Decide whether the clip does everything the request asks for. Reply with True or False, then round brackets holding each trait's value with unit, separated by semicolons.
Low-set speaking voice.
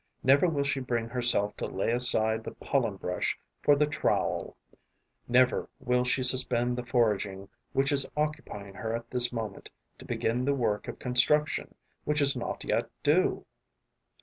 True (125 Hz)